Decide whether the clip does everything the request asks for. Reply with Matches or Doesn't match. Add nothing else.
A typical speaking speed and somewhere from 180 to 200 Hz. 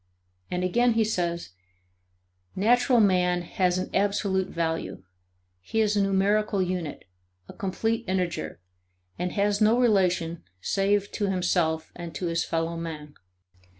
Doesn't match